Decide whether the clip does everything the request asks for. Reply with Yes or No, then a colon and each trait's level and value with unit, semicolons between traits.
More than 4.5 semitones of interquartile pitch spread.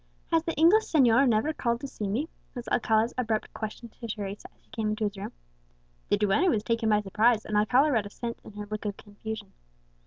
No: average, 2.8 semitones